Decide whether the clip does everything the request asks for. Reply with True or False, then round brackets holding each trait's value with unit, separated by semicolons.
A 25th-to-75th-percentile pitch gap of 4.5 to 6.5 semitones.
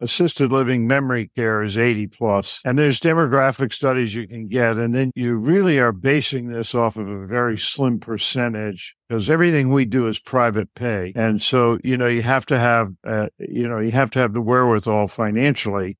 False (3.0 semitones)